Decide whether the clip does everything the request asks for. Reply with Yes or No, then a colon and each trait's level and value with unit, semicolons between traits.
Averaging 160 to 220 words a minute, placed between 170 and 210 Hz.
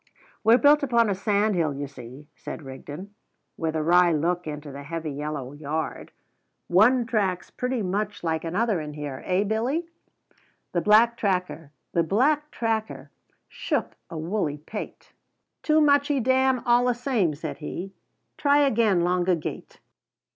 No: slow, 135 wpm; medium, 185 Hz